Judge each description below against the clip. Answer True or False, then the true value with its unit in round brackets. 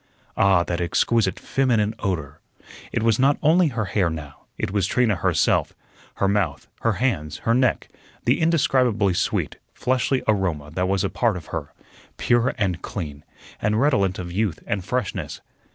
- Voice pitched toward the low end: True (100 Hz)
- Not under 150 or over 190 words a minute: True (160 wpm)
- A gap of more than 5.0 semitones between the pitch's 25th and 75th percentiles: True (5.5 semitones)